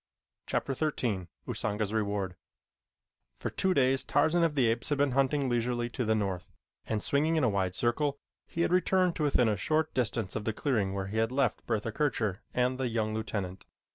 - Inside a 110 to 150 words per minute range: No, average, 195 wpm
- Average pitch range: Yes, average, 4.9 semitones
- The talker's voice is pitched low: Yes, low, 120 Hz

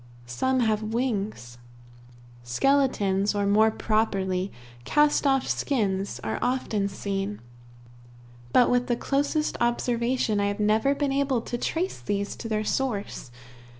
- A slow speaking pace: Yes, slow, 125 wpm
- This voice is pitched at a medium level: No, high, 220 Hz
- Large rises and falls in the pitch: No, average, 4.5 semitones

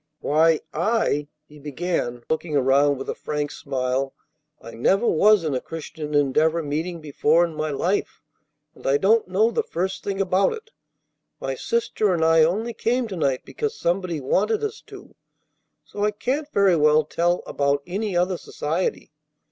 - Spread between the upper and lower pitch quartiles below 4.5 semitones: No, average, 5.2 semitones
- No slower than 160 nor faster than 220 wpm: Yes, average, 165 wpm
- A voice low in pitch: No, medium, 165 Hz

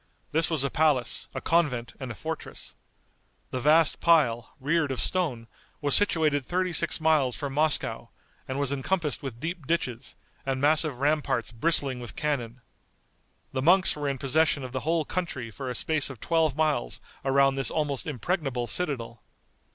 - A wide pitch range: No, average, 3.6 semitones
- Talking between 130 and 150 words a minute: No, average, 165 wpm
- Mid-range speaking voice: Yes, medium, 145 Hz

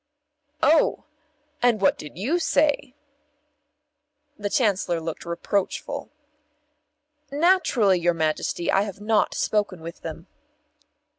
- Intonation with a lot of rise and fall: Yes, wide, 6.4 semitones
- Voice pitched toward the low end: No, high, 200 Hz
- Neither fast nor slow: No, slow, 100 wpm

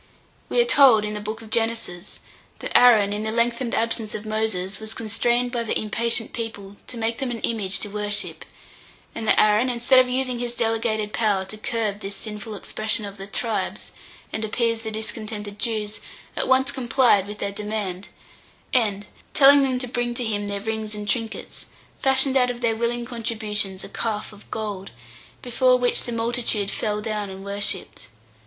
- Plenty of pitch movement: No, narrow, 2.4 semitones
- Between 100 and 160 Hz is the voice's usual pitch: No, high, 220 Hz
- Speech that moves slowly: No, average, 180 wpm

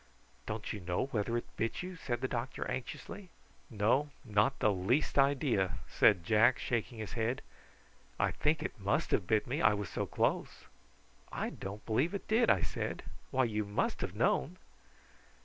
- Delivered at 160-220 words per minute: Yes, average, 170 wpm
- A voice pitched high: No, low, 115 Hz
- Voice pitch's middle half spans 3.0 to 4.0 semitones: No, average, 4.5 semitones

